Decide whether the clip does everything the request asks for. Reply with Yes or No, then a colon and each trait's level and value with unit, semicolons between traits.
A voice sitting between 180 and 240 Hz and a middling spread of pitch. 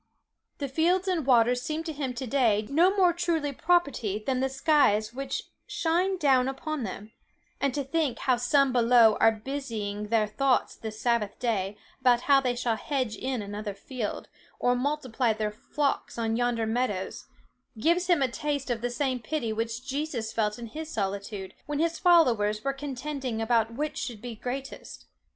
No: very high, 250 Hz; average, 4.4 semitones